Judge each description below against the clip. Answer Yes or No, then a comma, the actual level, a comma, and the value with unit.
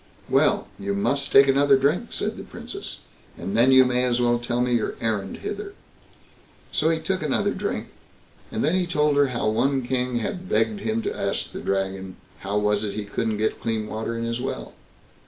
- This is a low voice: Yes, low, 125 Hz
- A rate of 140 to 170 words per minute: No, average, 200 wpm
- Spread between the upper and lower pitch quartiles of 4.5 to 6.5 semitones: Yes, average, 4.8 semitones